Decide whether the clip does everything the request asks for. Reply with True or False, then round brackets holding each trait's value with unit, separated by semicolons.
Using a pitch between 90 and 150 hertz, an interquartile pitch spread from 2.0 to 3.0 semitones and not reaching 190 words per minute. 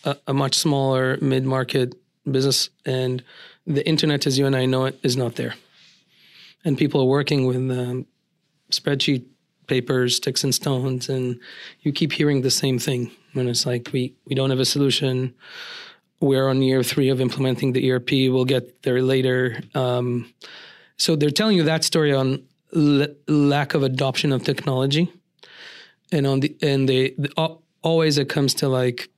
True (135 Hz; 2.7 semitones; 170 wpm)